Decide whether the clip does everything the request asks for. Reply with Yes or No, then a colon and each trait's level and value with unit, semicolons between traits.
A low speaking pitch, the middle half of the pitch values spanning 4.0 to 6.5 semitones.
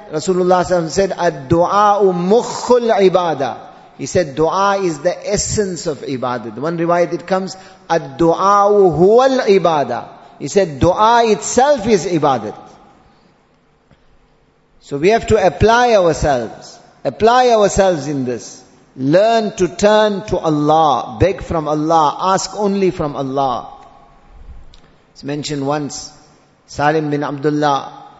No: medium, 175 Hz; average, 5.2 semitones